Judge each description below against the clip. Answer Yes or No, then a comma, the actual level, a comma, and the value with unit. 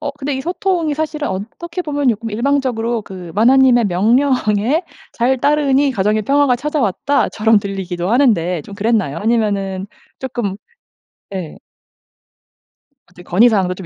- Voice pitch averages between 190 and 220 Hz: No, high, 230 Hz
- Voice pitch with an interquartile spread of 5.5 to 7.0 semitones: Yes, wide, 6.1 semitones